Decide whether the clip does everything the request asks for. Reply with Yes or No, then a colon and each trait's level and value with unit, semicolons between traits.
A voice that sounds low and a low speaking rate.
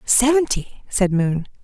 No: high, 215 Hz; slow, 110 wpm